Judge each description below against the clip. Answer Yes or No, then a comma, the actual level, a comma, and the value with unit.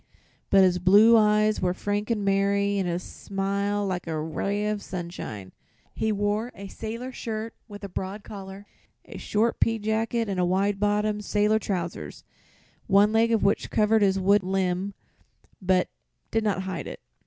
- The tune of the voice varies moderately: No, narrow, 2.0 semitones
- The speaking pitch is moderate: No, high, 200 Hz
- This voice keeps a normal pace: Yes, average, 160 wpm